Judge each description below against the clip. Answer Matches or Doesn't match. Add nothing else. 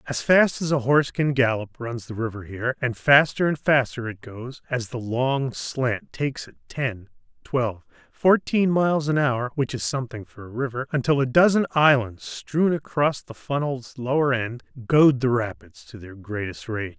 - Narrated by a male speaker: Matches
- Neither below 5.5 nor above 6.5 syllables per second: Doesn't match